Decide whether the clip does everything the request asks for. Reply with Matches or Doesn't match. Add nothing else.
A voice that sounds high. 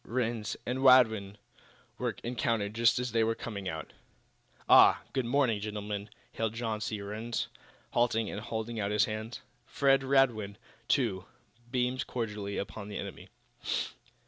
Doesn't match